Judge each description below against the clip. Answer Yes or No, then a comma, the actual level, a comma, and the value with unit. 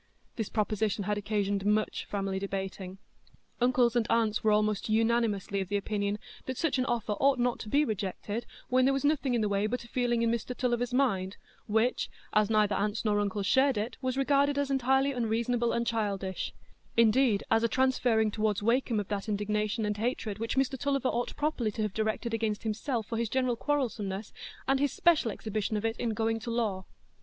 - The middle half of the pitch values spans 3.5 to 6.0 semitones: No, average, 3.1 semitones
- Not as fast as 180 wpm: No, average, 190 wpm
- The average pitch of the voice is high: Yes, high, 225 Hz